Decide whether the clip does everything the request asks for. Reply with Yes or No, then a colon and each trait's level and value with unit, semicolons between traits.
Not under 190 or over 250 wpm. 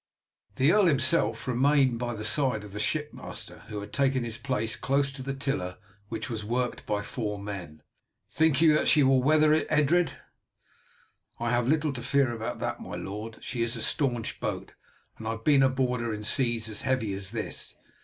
Yes: average, 195 wpm